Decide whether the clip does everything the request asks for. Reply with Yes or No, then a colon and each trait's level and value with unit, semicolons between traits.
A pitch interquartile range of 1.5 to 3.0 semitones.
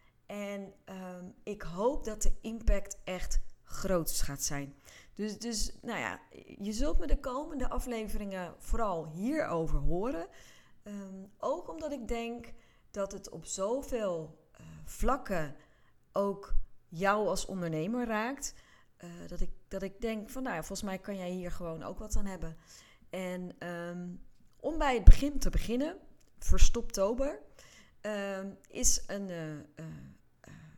No: average, 4.8 semitones